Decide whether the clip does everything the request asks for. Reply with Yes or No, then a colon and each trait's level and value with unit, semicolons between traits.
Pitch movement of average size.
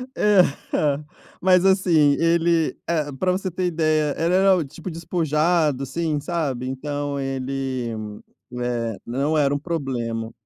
Yes: average, 4.0 semitones